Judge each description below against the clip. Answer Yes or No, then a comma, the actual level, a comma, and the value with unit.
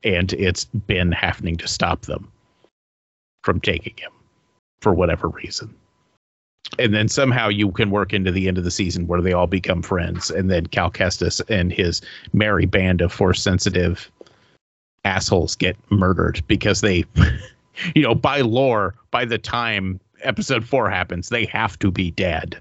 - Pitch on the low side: Yes, very low, 95 Hz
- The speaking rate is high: No, average, 160 wpm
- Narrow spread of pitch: No, average, 3.1 semitones